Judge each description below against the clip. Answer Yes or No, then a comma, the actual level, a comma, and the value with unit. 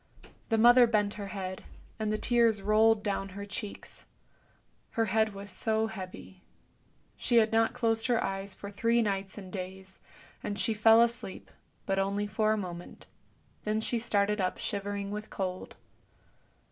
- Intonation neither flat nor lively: No, narrow, 2.3 semitones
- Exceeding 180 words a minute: No, average, 160 wpm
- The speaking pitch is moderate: No, high, 210 Hz